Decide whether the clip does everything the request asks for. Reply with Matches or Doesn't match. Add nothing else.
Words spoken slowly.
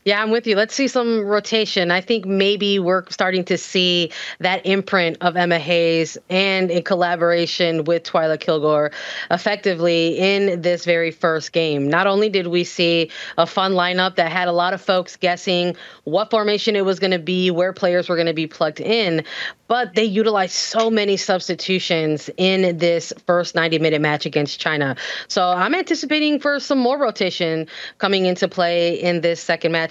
Doesn't match